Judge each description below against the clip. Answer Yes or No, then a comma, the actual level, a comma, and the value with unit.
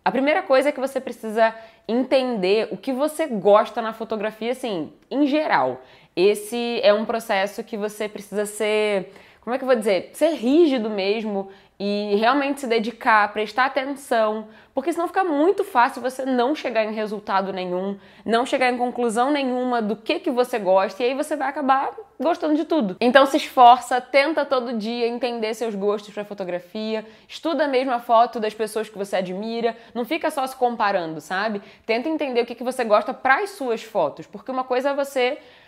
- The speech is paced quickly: Yes, fast, 190 wpm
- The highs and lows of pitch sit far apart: No, average, 3.9 semitones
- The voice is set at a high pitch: Yes, high, 235 Hz